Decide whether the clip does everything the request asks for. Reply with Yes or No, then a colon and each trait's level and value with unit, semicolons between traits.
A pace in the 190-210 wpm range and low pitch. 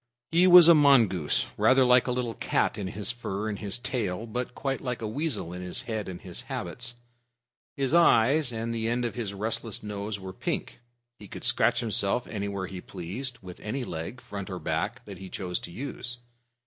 Yes: average, 200 wpm; low, 110 Hz